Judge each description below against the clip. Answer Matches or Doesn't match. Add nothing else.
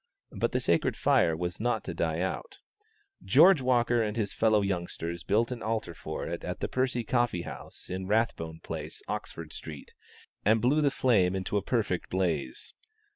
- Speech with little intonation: Doesn't match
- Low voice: Matches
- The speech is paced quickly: Doesn't match